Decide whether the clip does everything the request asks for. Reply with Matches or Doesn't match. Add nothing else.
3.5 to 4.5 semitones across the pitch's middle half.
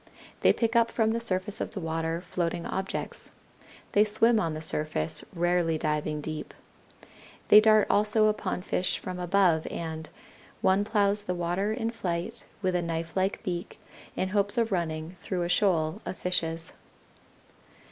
Matches